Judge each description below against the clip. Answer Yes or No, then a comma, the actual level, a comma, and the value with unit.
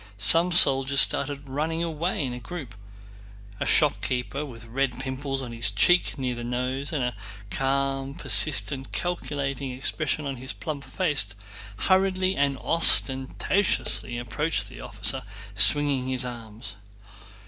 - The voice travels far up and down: No, average, 3.3 semitones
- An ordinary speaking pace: No, slow, 130 wpm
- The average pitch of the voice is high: No, low, 135 Hz